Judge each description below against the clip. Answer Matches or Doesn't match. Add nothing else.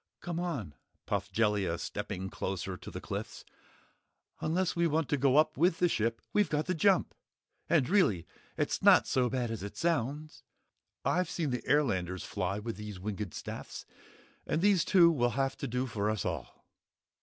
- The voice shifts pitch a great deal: Matches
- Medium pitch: Doesn't match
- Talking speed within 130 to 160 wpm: Doesn't match